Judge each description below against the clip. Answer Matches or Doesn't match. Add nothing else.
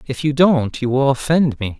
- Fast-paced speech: Matches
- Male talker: Matches